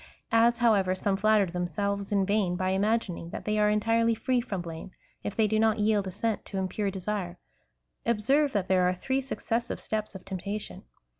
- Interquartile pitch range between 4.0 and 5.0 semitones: No, average, 2.9 semitones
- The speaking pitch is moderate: No, high, 205 Hz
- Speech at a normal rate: Yes, average, 190 wpm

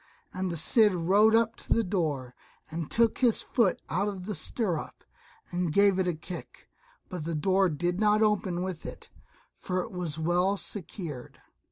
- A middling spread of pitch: Yes, average, 3.6 semitones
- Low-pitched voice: No, medium, 185 Hz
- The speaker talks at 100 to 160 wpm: No, average, 175 wpm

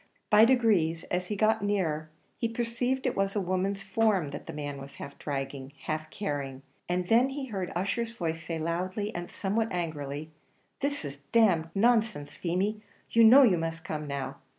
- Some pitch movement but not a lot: No, wide, 6.0 semitones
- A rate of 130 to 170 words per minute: No, average, 180 wpm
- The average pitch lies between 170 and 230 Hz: Yes, medium, 185 Hz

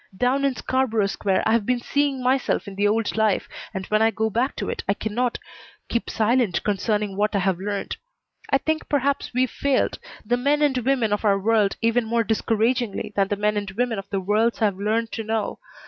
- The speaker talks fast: Yes, fast, 210 wpm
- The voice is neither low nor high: No, high, 225 Hz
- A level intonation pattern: No, average, 3.3 semitones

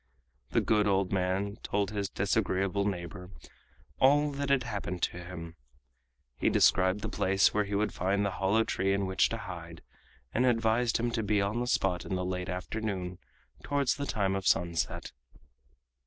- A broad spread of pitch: No, average, 3.2 semitones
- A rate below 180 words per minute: Yes, average, 170 wpm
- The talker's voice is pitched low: Yes, low, 100 Hz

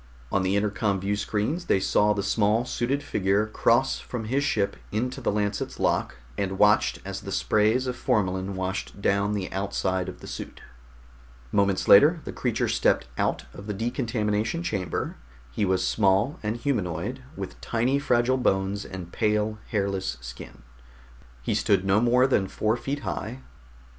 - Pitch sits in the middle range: No, low, 105 Hz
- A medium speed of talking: Yes, average, 160 wpm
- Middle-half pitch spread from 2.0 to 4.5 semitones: Yes, average, 3.5 semitones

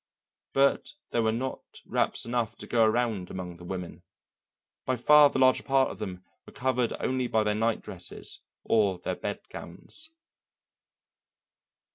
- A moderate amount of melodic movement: Yes, average, 4.6 semitones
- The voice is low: Yes, low, 115 Hz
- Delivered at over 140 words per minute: Yes, average, 150 wpm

